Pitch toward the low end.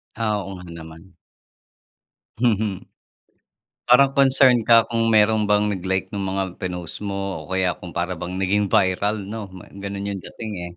Yes: low, 100 Hz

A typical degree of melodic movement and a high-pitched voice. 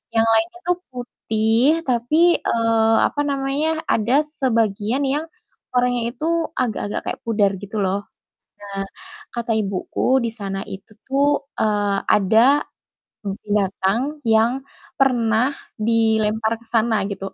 Yes: average, 4.0 semitones; high, 230 Hz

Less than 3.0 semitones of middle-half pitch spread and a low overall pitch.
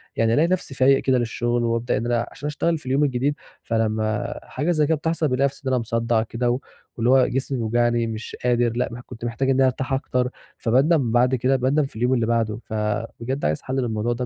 Yes: narrow, 2.5 semitones; low, 125 Hz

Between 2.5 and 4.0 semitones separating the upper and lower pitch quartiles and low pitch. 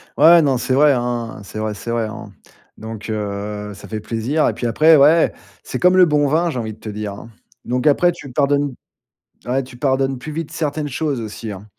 No: average, 5.3 semitones; low, 125 Hz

